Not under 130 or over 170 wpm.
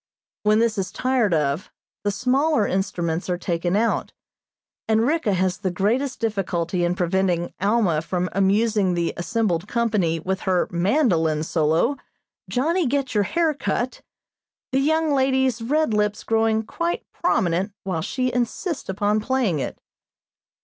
Yes: average, 140 wpm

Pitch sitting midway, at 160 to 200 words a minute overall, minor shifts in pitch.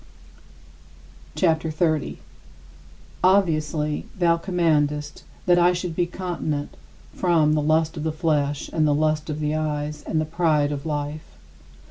No: medium, 155 Hz; average, 140 wpm; narrow, 2.0 semitones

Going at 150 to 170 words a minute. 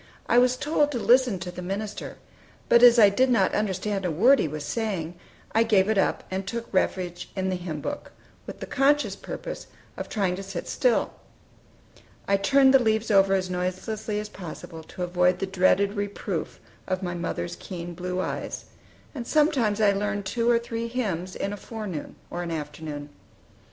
No: average, 185 wpm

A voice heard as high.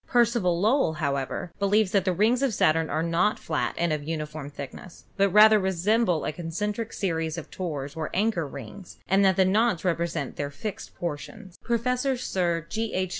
No: medium, 180 Hz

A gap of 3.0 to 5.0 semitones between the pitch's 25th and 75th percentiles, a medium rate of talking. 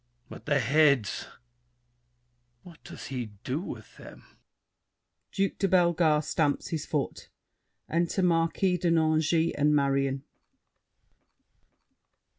No: average, 3.5 semitones; slow, 100 wpm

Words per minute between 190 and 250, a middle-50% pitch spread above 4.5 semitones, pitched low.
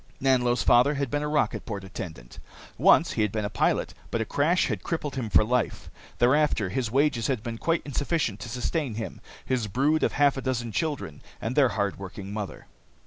Yes: average, 200 wpm; average, 5.0 semitones; low, 125 Hz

